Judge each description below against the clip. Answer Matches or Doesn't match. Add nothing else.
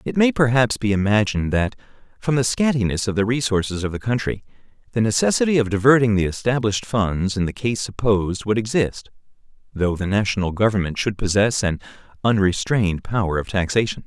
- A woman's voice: Doesn't match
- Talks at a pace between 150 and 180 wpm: Matches